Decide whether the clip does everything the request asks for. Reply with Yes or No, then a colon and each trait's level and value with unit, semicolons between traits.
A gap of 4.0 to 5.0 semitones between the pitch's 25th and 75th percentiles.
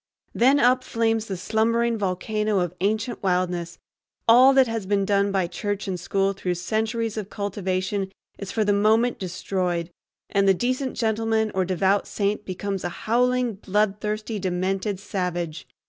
No: average, 3.0 semitones